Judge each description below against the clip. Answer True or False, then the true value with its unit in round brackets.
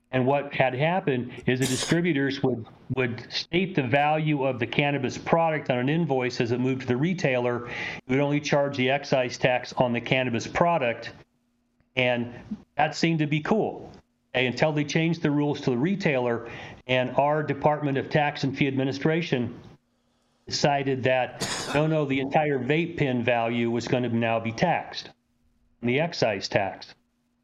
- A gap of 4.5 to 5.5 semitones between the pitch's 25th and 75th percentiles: False (3.5 semitones)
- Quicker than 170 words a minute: False (165 wpm)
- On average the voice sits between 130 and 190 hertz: True (135 Hz)